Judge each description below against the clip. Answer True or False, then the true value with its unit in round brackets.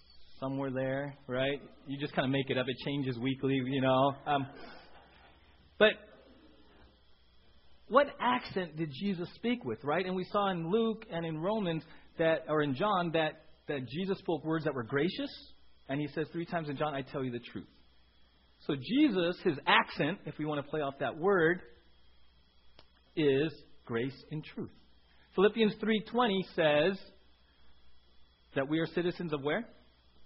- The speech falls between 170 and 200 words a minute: False (160 wpm)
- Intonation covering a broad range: True (8.7 semitones)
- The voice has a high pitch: False (145 Hz)